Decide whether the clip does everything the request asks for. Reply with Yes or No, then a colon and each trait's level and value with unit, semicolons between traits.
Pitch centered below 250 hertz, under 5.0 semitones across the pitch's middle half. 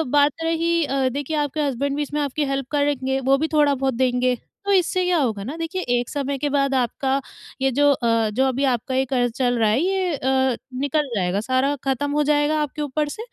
No: very high, 275 Hz; narrow, 2.5 semitones